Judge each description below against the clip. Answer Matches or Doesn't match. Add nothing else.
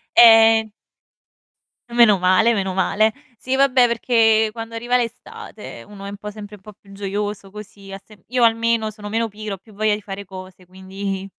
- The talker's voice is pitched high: Matches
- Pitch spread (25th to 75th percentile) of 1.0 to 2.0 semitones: Doesn't match